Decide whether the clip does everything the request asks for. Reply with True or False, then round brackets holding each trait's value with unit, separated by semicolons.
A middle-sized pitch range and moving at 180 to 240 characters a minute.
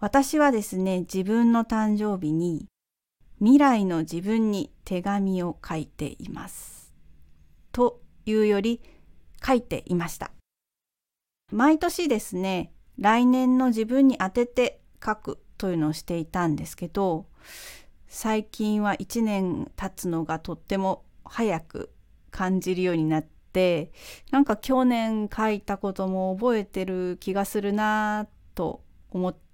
True (3.8 semitones; 235 characters per minute)